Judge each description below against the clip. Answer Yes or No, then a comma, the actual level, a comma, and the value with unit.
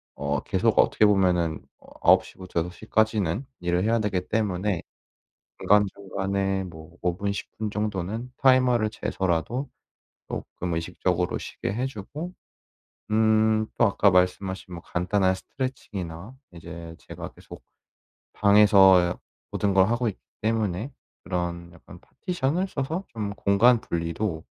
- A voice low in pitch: Yes, low, 100 Hz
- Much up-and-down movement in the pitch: No, average, 3.7 semitones